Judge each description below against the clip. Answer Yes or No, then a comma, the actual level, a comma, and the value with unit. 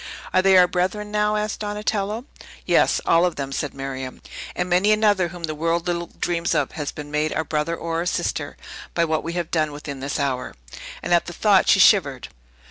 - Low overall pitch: No, medium, 170 Hz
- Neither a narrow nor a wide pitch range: Yes, average, 4.0 semitones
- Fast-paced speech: Yes, fast, 210 wpm